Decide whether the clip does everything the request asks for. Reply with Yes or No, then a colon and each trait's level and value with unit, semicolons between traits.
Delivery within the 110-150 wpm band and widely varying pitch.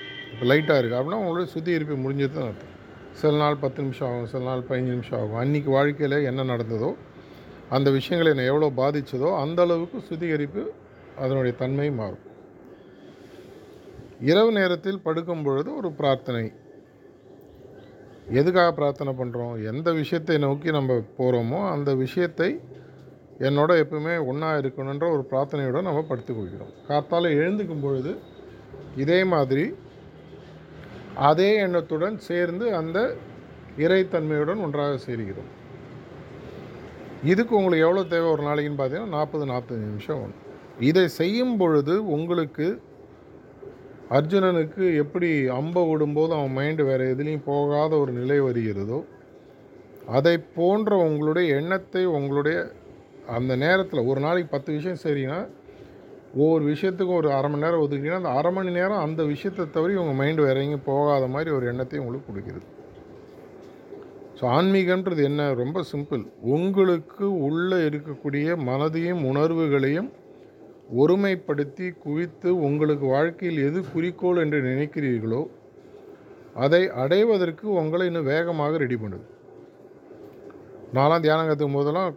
No: average, 115 wpm; average, 4.2 semitones